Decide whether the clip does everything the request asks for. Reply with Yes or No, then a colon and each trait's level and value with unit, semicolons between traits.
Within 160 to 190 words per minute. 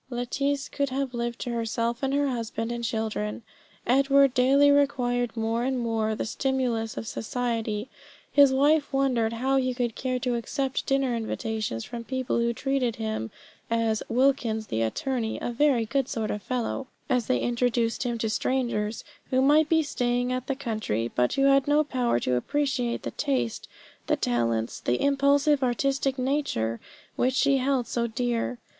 Yes: average, 165 wpm